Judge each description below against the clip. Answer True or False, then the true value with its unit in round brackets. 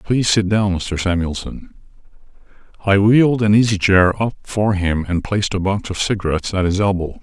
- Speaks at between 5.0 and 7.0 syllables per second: True (5.4 syllables/s)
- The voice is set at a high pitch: False (100 Hz)